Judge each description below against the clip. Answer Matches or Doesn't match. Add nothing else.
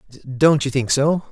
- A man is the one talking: Matches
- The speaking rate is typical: Matches